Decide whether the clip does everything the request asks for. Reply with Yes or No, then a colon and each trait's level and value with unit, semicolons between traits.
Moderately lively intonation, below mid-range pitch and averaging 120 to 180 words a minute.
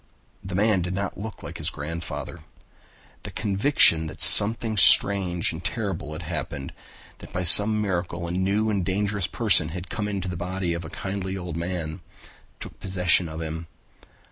Yes: average, 3.0 semitones; very low, 90 Hz; average, 170 wpm